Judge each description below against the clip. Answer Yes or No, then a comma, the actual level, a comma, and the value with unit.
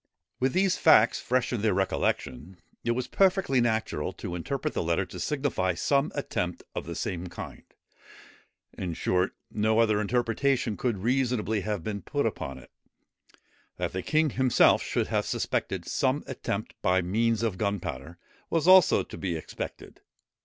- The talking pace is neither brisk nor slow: Yes, average, 155 wpm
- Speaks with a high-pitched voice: No, low, 110 Hz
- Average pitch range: No, wide, 6.1 semitones